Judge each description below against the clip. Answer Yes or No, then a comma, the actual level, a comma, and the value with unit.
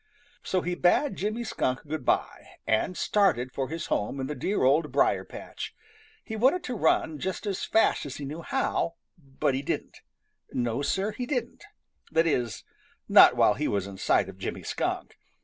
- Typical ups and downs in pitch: No, wide, 7.4 semitones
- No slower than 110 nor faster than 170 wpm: No, average, 185 wpm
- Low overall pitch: No, medium, 155 Hz